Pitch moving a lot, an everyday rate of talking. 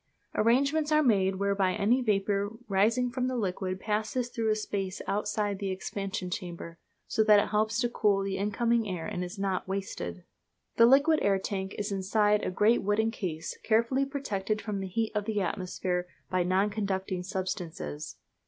No: average, 2.8 semitones; average, 170 wpm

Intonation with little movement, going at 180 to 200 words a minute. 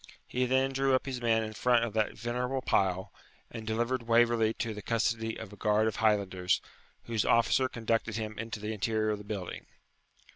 Yes: narrow, 1.9 semitones; average, 190 wpm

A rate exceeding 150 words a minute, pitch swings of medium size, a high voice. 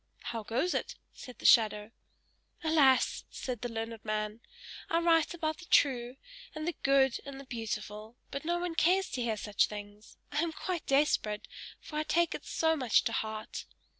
No: average, 180 wpm; wide, 6.4 semitones; very high, 260 Hz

